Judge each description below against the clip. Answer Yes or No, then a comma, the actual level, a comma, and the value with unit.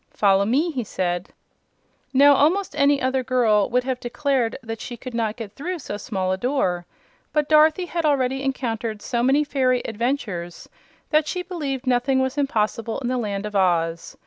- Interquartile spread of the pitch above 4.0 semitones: Yes, average, 4.9 semitones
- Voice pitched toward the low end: No, very high, 250 Hz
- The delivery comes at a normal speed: Yes, average, 180 wpm